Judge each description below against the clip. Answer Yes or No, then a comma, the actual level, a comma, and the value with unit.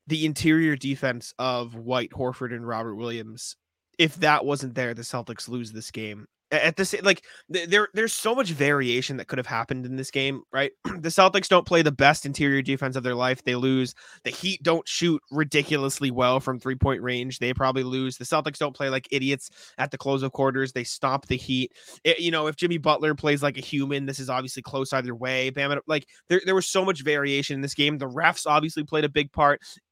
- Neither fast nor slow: No, fast, 220 wpm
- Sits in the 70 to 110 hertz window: No, low, 135 Hz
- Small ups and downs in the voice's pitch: No, average, 3.2 semitones